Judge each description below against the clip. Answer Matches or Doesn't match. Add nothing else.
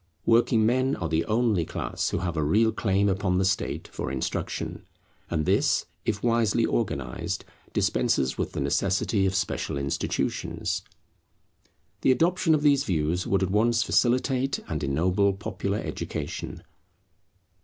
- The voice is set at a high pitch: Doesn't match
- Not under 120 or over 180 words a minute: Matches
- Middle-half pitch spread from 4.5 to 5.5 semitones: Matches